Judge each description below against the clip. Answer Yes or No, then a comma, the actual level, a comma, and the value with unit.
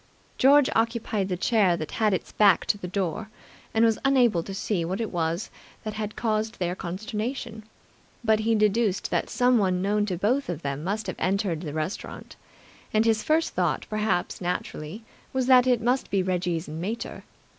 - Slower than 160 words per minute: No, average, 175 wpm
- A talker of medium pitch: No, high, 210 Hz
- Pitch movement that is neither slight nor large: Yes, average, 3.9 semitones